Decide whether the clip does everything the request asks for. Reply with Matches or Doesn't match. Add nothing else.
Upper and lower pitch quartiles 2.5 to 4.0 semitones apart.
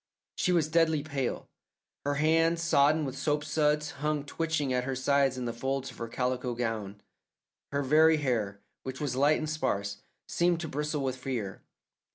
Matches